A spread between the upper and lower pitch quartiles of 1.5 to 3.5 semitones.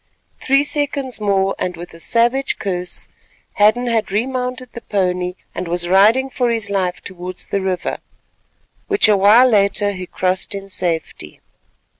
No: average, 4.9 semitones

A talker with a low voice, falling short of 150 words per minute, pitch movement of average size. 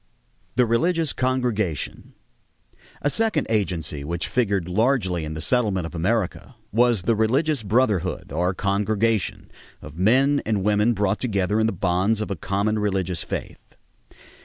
Yes: low, 105 Hz; average, 140 wpm; average, 4.5 semitones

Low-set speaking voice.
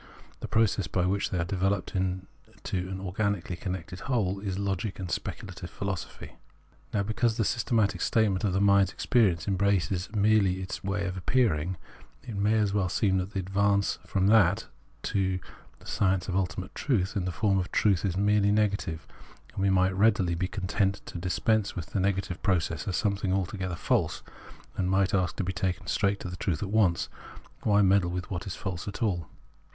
Yes: very low, 95 Hz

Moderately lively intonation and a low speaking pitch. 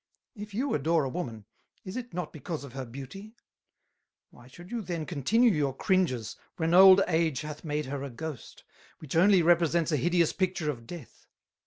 No: average, 4.9 semitones; medium, 165 Hz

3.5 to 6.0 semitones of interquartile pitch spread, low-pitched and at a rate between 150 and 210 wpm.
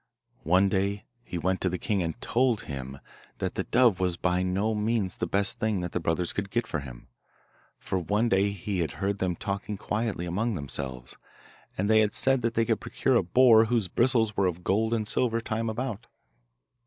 Yes: average, 3.8 semitones; low, 100 Hz; fast, 205 wpm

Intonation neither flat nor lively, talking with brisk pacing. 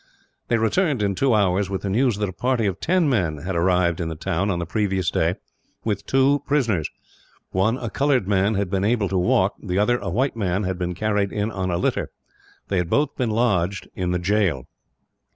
Yes: average, 4.1 semitones; fast, 215 wpm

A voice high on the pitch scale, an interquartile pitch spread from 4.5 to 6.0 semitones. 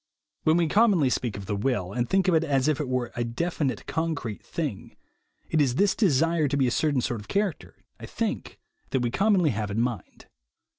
No: medium, 140 Hz; wide, 5.5 semitones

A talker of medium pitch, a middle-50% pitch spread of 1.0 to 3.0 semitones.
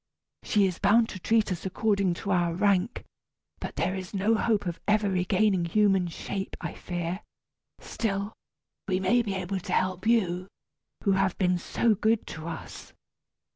No: high, 195 Hz; narrow, 2.6 semitones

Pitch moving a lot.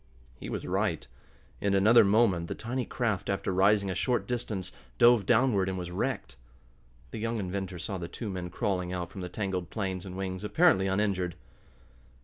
No: average, 3.1 semitones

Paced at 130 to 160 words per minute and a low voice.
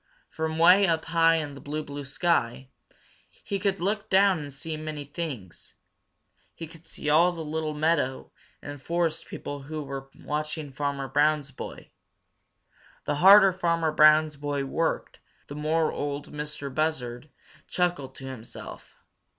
No: average, 145 wpm; medium, 155 Hz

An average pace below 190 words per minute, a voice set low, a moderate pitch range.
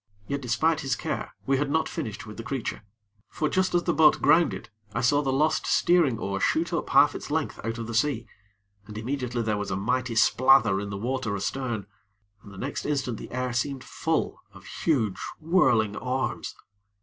No: average, 195 wpm; low, 125 Hz; average, 4.4 semitones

